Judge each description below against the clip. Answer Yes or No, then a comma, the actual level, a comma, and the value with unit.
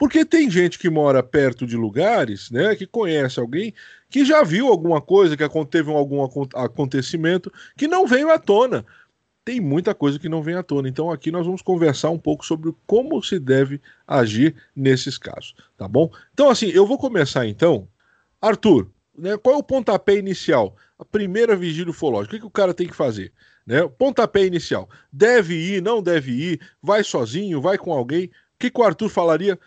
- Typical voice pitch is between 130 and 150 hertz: No, medium, 175 Hz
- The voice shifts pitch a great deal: Yes, wide, 5.9 semitones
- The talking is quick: Yes, fast, 190 wpm